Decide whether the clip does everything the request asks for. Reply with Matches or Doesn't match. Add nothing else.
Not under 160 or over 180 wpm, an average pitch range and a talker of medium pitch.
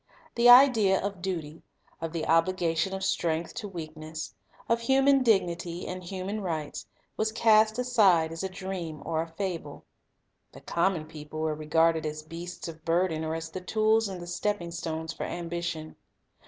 Matches